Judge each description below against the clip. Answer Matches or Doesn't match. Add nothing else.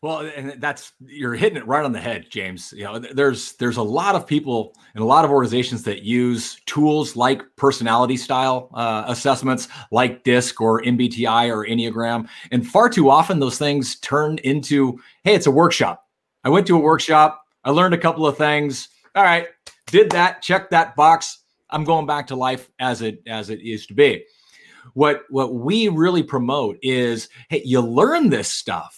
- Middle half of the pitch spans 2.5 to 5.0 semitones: Matches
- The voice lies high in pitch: Doesn't match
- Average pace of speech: Matches